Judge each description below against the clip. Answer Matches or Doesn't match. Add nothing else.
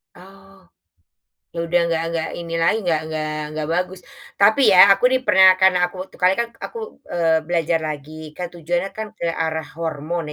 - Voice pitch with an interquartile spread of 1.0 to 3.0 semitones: Matches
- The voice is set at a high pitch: Doesn't match